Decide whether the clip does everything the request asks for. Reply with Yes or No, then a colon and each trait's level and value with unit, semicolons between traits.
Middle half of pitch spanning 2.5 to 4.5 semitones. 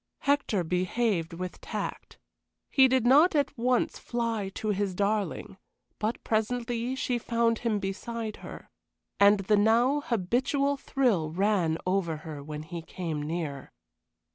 No: average, 5.1 semitones